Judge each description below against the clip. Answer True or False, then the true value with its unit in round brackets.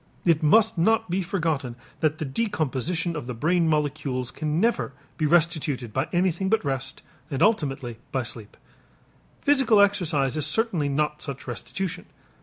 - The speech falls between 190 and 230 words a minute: False (150 wpm)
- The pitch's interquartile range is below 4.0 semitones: False (5.3 semitones)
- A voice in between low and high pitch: True (155 Hz)